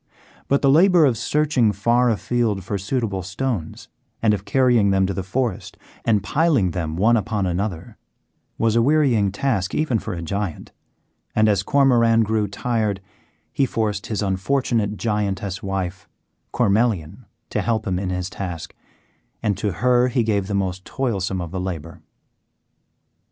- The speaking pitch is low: Yes, low, 105 Hz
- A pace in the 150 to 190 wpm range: Yes, average, 155 wpm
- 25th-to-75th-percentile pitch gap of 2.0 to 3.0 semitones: No, average, 4.1 semitones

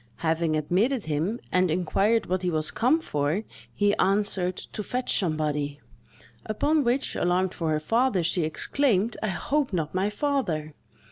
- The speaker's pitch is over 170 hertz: Yes, medium, 185 Hz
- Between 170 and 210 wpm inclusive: No, average, 150 wpm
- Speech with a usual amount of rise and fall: No, wide, 6.3 semitones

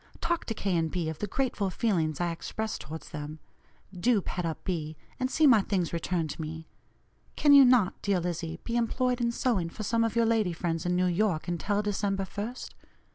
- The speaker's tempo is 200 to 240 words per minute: Yes, fast, 205 wpm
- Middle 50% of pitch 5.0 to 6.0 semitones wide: Yes, wide, 5.5 semitones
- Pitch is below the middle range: No, high, 190 Hz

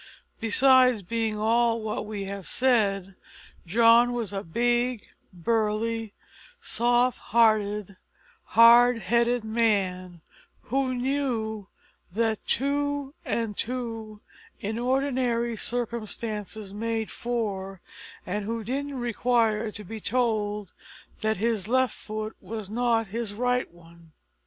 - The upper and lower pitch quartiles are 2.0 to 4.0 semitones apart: Yes, narrow, 2.5 semitones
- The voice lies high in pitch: Yes, high, 225 Hz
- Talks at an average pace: No, slow, 110 wpm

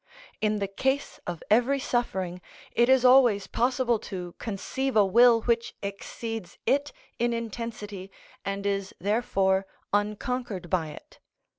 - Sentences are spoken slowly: Yes, slow, 130 wpm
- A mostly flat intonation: No, average, 3.7 semitones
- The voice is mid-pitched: No, high, 220 Hz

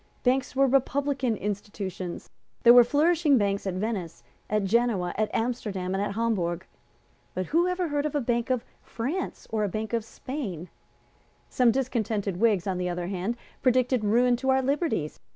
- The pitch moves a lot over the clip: No, average, 5.0 semitones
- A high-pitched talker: Yes, high, 230 Hz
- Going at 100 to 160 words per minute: No, average, 170 wpm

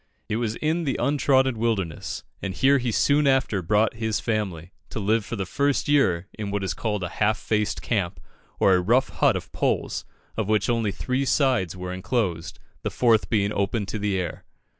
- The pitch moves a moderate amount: Yes, average, 4.5 semitones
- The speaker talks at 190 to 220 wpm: Yes, average, 195 wpm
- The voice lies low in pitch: Yes, low, 110 Hz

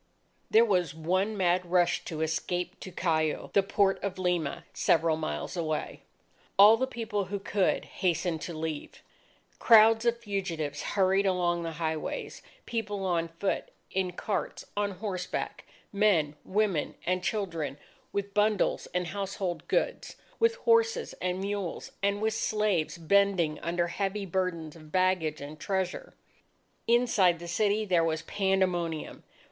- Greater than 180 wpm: No, average, 140 wpm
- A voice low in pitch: No, medium, 185 Hz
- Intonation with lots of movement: No, average, 3.3 semitones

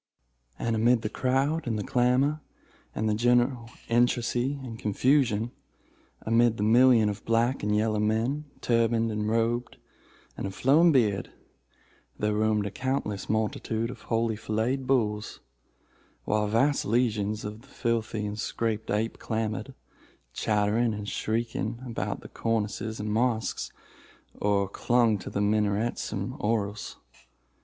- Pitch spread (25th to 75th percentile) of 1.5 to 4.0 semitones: Yes, narrow, 2.4 semitones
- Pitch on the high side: No, low, 115 Hz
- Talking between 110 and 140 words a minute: Yes, slow, 135 wpm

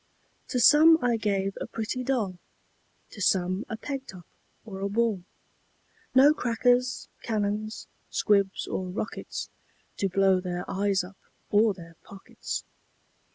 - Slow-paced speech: Yes, slow, 130 wpm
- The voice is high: Yes, high, 205 Hz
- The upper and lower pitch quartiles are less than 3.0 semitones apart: No, average, 3.7 semitones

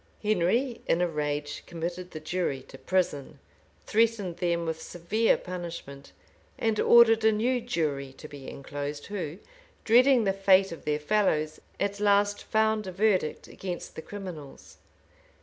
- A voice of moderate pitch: Yes, medium, 180 Hz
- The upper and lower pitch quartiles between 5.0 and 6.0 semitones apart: Yes, wide, 5.4 semitones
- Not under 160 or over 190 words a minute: No, average, 145 wpm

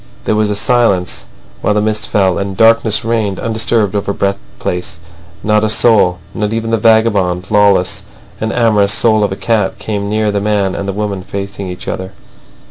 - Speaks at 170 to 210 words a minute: Yes, average, 185 wpm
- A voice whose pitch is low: Yes, low, 105 Hz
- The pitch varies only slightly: Yes, narrow, 1.9 semitones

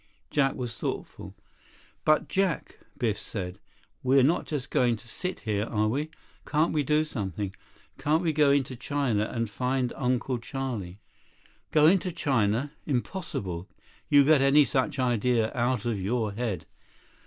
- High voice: No, low, 125 Hz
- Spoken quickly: No, average, 145 wpm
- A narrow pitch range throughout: No, average, 4.8 semitones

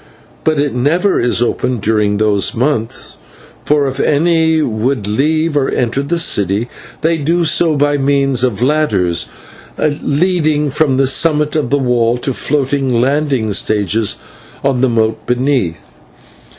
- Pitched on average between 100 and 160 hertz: Yes, low, 135 Hz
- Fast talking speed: No, average, 140 wpm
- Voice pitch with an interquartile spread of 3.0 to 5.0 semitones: Yes, average, 4.4 semitones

